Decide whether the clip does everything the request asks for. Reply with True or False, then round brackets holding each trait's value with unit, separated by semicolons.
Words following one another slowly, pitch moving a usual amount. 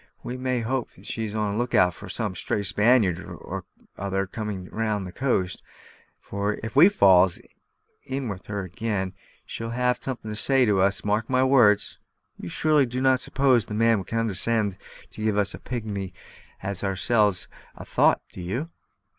False (175 wpm; 4.2 semitones)